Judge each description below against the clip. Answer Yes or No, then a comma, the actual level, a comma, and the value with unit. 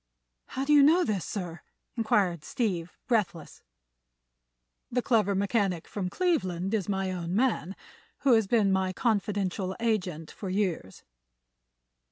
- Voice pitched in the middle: No, high, 195 Hz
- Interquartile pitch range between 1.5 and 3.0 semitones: No, average, 4.0 semitones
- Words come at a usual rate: No, slow, 130 wpm